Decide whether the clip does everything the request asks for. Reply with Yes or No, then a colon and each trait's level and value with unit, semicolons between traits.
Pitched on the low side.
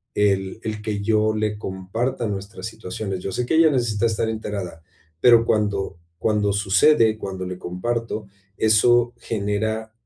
Yes: low, 105 Hz